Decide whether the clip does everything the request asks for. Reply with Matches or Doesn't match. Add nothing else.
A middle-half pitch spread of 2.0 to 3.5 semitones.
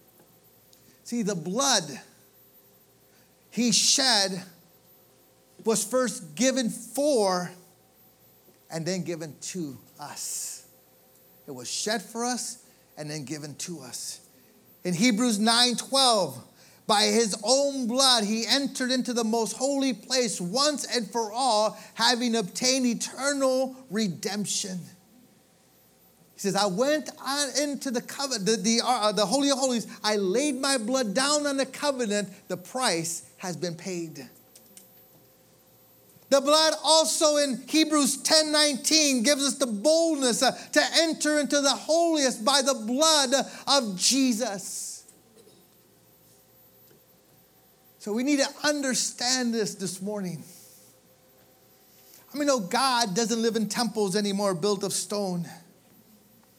Doesn't match